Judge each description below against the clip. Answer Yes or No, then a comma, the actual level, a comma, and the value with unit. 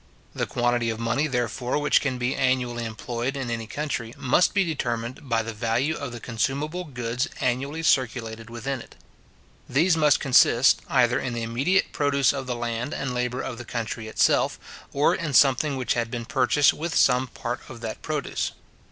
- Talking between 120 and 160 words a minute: No, average, 180 wpm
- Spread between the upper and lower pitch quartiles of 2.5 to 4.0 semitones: Yes, average, 3.0 semitones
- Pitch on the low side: Yes, low, 125 Hz